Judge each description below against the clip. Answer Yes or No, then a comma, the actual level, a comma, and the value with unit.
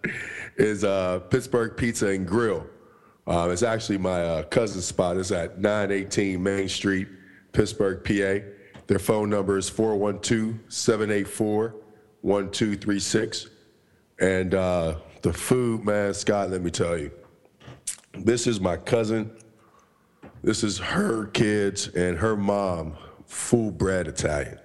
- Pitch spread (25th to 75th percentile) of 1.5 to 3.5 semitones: Yes, average, 2.9 semitones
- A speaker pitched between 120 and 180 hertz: No, low, 100 Hz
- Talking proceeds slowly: Yes, slow, 125 wpm